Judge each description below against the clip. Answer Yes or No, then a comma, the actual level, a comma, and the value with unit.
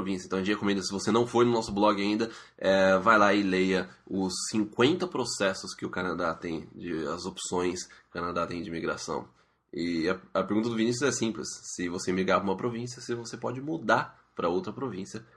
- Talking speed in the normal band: No, fast, 205 wpm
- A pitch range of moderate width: Yes, average, 3.6 semitones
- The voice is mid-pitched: No, low, 100 Hz